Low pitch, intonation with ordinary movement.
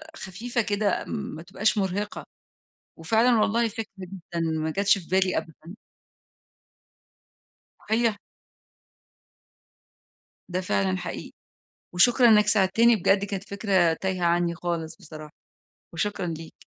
No: high, 190 Hz; average, 3.8 semitones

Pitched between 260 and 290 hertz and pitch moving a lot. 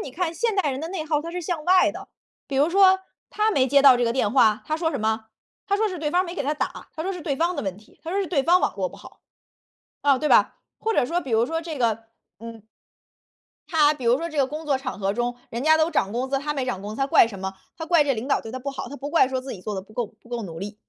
Yes: very high, 280 Hz; wide, 5.7 semitones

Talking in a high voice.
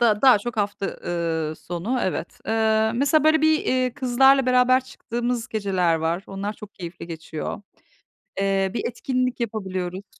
Yes: high, 220 Hz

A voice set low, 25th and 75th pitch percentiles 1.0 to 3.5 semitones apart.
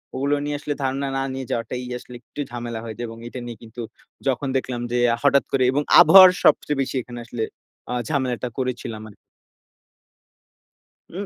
Yes: low, 130 Hz; average, 2.8 semitones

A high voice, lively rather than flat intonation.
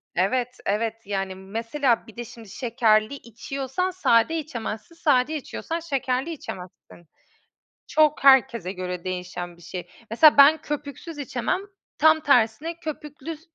Yes: very high, 250 Hz; wide, 5.9 semitones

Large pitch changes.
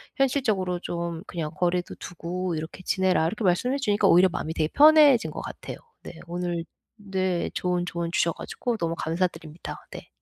No: average, 2.9 semitones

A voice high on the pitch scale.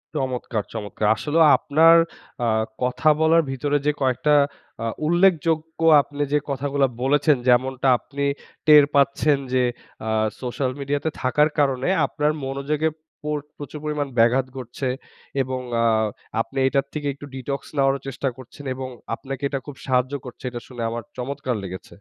No: medium, 140 Hz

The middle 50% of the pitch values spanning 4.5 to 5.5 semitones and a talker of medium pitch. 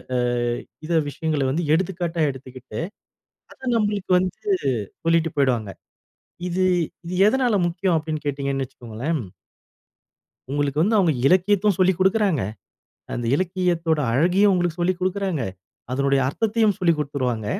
Yes: average, 5.1 semitones; medium, 170 Hz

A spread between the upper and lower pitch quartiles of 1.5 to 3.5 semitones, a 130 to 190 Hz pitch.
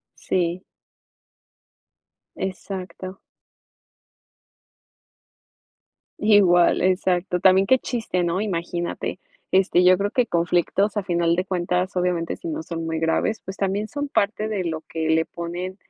Yes: narrow, 2.4 semitones; medium, 185 Hz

